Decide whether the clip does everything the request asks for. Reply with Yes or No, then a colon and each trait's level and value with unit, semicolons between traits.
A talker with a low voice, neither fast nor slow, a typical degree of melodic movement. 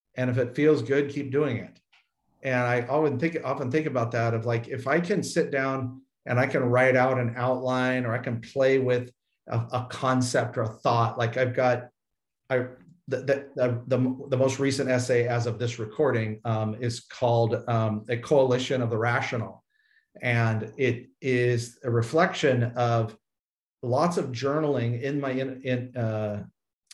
No: low, 125 Hz; average, 175 wpm; narrow, 2.1 semitones